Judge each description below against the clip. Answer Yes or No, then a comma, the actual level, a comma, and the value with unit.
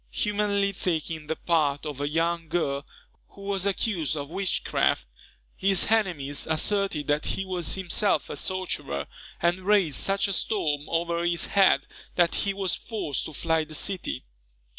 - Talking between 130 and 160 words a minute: Yes, average, 155 wpm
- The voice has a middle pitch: Yes, medium, 170 Hz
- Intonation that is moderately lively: Yes, average, 4.2 semitones